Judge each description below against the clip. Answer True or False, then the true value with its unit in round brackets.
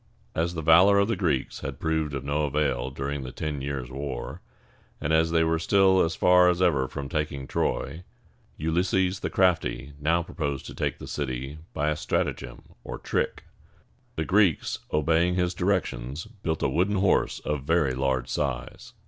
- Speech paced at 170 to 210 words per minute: True (175 wpm)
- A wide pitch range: False (4.3 semitones)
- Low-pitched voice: True (80 Hz)